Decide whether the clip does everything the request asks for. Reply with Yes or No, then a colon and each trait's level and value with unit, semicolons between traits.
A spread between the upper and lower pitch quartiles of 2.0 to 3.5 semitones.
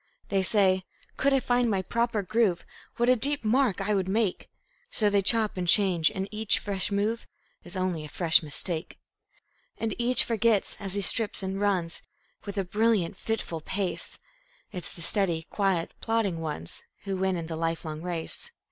No: average, 4.0 semitones